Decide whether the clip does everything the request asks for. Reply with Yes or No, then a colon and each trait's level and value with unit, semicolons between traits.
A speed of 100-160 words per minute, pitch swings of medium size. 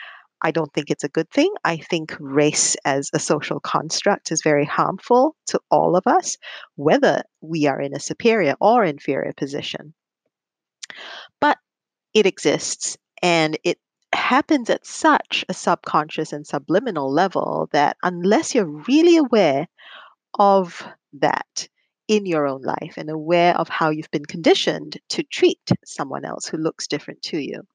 No: average, 150 wpm; wide, 6.4 semitones